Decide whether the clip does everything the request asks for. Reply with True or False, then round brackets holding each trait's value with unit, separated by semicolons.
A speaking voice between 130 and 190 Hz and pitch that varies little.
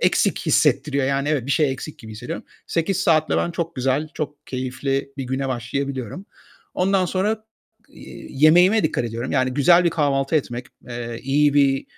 False (140 Hz; 3.5 semitones)